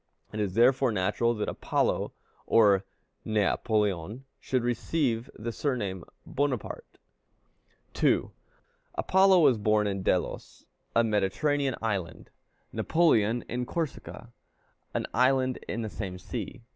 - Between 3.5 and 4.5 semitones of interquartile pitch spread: Yes, average, 3.9 semitones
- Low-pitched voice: Yes, low, 115 Hz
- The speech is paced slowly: Yes, slow, 120 wpm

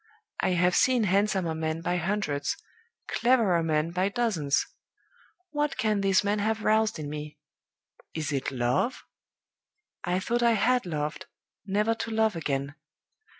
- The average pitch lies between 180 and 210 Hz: Yes, high, 190 Hz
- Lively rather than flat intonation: Yes, wide, 5.7 semitones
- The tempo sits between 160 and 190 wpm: No, average, 140 wpm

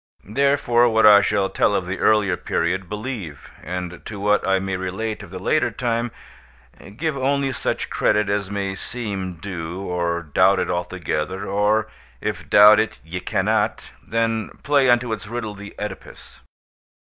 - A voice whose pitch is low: Yes, low, 100 Hz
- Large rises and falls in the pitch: No, average, 3.5 semitones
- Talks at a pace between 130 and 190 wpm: Yes, average, 160 wpm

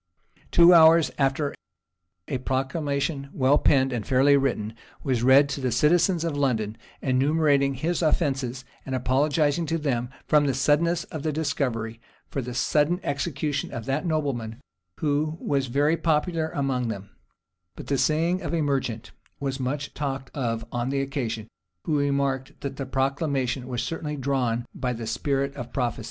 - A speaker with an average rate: Yes, average, 160 wpm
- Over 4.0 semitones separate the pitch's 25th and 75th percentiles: No, average, 2.8 semitones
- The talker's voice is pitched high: No, medium, 140 Hz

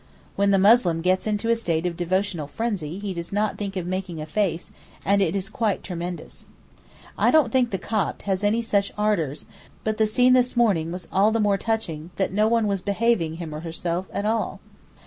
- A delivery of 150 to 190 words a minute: No, fast, 205 wpm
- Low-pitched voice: No, high, 195 Hz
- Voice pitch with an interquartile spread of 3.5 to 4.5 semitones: Yes, average, 3.8 semitones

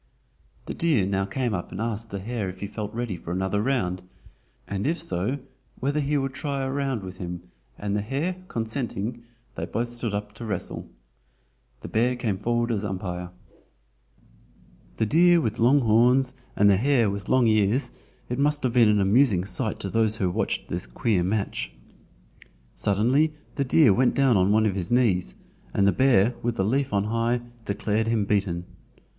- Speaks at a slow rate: No, average, 185 wpm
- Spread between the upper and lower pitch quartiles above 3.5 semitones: Yes, average, 4.3 semitones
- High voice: No, low, 110 Hz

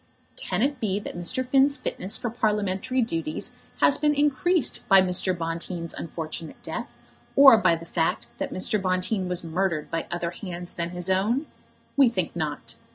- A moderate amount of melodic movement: No, wide, 5.7 semitones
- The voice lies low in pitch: No, medium, 185 Hz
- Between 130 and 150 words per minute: No, average, 165 wpm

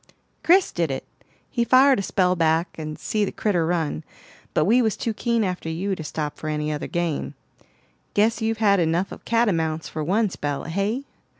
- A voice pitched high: No, medium, 180 Hz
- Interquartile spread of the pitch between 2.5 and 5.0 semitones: No, wide, 5.5 semitones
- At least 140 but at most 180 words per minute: No, average, 190 wpm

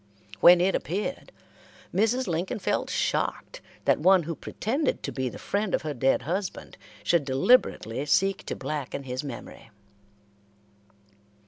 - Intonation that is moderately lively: No, wide, 6.1 semitones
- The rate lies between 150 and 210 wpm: No, slow, 135 wpm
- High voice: No, medium, 170 Hz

